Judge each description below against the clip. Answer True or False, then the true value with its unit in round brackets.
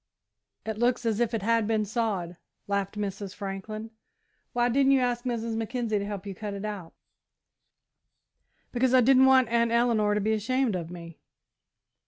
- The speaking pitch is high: True (220 Hz)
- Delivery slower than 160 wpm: False (165 wpm)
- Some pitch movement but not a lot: True (3.0 semitones)